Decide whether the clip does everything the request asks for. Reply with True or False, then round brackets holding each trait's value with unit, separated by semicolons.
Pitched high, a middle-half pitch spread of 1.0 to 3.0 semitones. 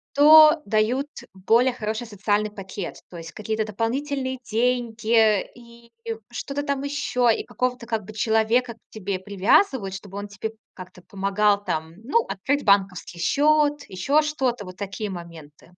False (220 Hz; 4.4 semitones)